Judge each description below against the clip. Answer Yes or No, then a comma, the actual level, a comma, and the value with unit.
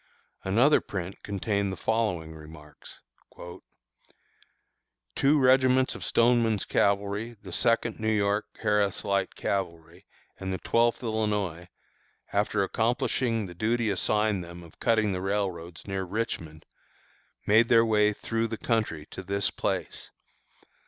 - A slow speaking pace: Yes, slow, 125 wpm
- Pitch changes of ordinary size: Yes, average, 3.3 semitones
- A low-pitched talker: Yes, low, 105 Hz